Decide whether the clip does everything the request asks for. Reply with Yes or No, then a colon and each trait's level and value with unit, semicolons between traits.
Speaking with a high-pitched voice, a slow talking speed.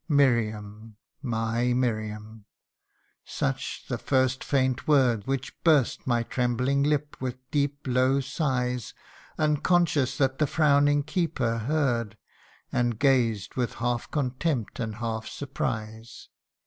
No: low, 125 Hz; slow, 120 wpm